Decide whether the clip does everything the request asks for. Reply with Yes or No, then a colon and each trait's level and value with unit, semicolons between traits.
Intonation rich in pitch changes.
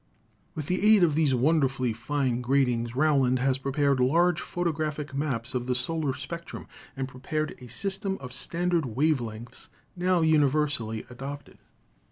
No: average, 3.9 semitones